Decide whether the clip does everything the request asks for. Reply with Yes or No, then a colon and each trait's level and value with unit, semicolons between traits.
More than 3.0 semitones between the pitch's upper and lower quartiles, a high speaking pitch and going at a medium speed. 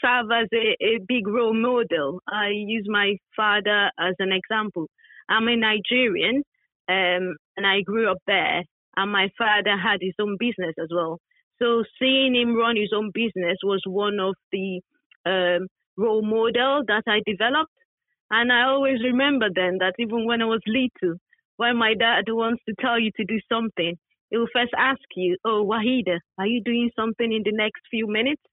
Yes: average, 3.4 semitones; high, 220 Hz; average, 180 wpm